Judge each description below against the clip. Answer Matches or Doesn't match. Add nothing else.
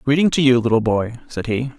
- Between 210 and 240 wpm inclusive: Matches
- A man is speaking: Matches